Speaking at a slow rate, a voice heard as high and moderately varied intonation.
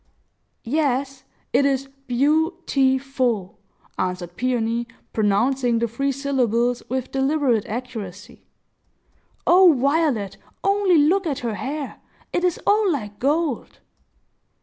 Yes: slow, 110 wpm; very high, 265 Hz; average, 4.1 semitones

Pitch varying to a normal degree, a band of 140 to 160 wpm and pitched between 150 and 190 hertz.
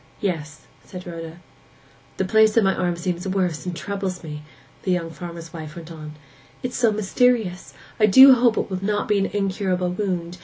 No: average, 3.3 semitones; average, 190 wpm; medium, 185 Hz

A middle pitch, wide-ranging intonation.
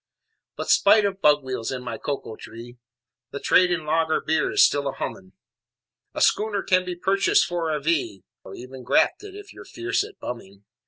Yes: medium, 155 Hz; wide, 7.4 semitones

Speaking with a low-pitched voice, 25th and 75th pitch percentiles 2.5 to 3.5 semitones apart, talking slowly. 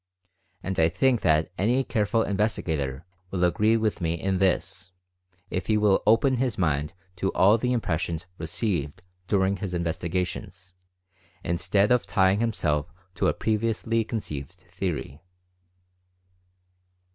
No: very low, 95 Hz; average, 4.3 semitones; slow, 125 wpm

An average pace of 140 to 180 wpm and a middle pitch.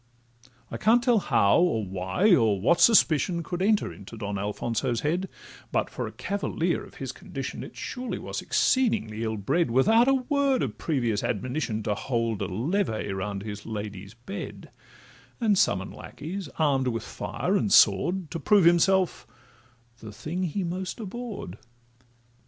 Yes: average, 155 wpm; medium, 150 Hz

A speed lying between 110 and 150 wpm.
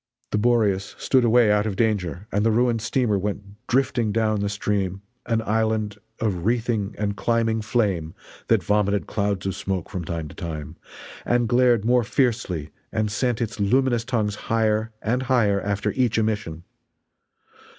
No: average, 160 wpm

